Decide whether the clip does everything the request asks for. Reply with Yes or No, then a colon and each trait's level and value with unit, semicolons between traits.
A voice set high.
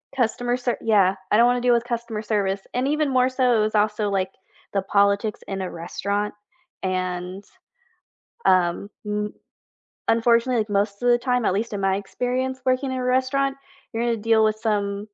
Yes: high, 220 Hz